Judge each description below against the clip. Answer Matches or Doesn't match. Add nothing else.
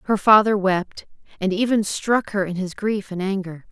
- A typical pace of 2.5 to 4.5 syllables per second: Doesn't match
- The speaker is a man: Doesn't match